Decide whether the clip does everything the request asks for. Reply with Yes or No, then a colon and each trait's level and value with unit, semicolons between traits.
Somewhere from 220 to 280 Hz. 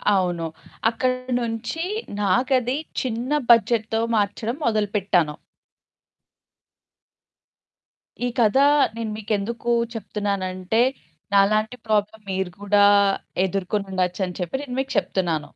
No: high, 210 Hz